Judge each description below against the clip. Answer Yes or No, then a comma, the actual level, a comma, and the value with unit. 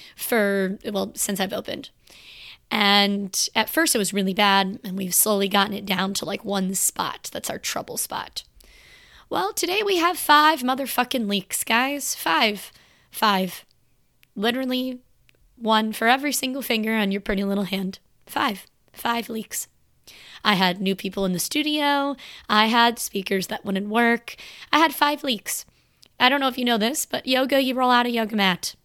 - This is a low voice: No, high, 220 Hz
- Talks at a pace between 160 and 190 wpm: Yes, average, 170 wpm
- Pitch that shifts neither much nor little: Yes, average, 4.7 semitones